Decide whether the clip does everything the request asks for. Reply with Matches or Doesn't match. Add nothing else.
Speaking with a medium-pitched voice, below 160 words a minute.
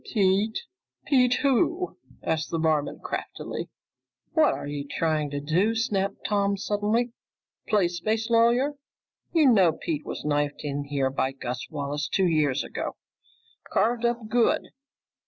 Doesn't match